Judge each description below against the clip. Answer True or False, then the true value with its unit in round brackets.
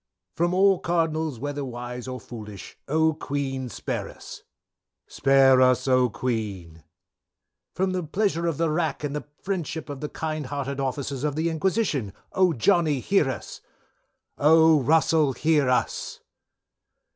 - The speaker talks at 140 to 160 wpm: True (145 wpm)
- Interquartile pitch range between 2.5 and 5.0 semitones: True (4.1 semitones)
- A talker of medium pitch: True (145 Hz)